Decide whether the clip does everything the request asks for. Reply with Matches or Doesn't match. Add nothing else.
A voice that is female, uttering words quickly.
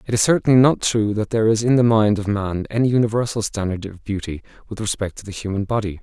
Doesn't match